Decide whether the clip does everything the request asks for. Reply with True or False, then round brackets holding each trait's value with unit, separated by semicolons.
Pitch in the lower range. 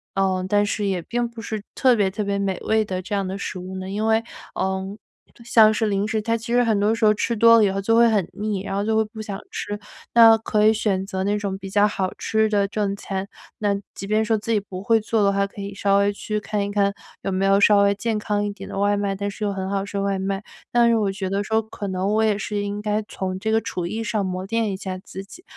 False (205 Hz)